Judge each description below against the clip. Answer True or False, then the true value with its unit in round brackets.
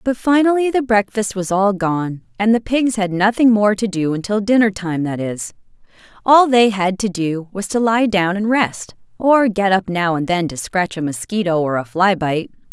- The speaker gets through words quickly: True (210 wpm)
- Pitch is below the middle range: False (200 Hz)